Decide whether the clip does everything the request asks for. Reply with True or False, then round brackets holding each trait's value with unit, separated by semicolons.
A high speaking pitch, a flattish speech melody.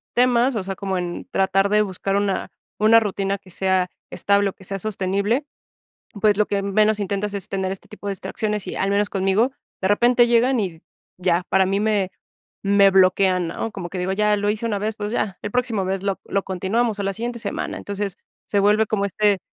True (200 Hz; 1.8 semitones)